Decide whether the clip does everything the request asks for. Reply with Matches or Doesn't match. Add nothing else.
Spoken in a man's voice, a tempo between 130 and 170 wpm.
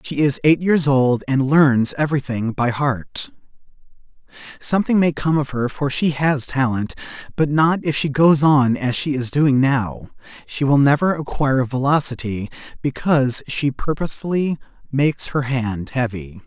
Matches